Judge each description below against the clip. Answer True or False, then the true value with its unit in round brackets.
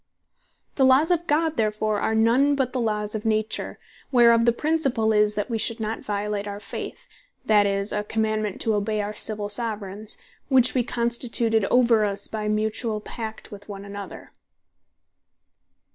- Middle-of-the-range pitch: False (220 Hz)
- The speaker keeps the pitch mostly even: True (2.2 semitones)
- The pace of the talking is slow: False (160 wpm)